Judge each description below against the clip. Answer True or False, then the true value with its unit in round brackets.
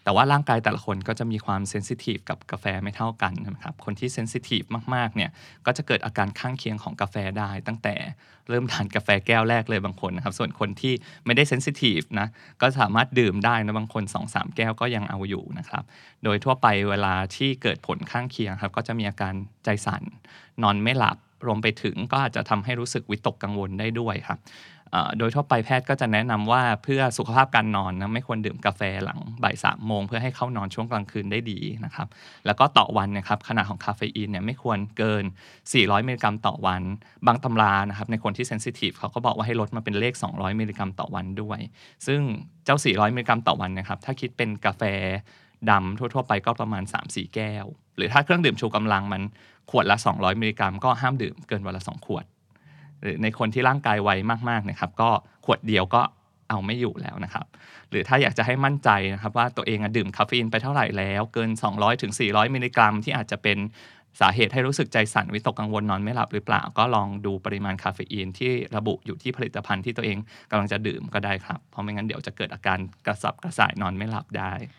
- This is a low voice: True (110 Hz)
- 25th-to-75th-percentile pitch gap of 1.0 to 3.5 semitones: True (3.0 semitones)